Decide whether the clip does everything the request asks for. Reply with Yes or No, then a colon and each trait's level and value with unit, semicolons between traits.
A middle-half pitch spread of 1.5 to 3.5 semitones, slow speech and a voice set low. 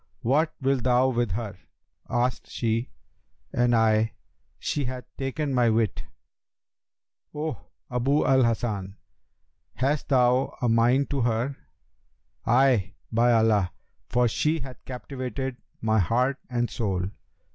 Yes: average, 2.8 semitones; slow, 120 wpm; low, 120 Hz